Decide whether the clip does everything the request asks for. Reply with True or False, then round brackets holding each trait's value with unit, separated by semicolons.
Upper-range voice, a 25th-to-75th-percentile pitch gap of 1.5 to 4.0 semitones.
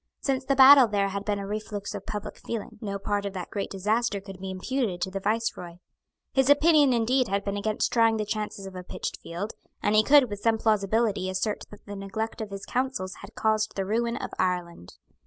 True (210 Hz; 2.8 semitones)